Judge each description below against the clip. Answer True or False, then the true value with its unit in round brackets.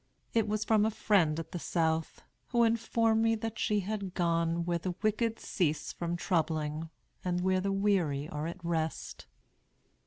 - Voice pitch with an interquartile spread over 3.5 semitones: True (4.6 semitones)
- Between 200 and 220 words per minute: False (165 wpm)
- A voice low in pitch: False (180 Hz)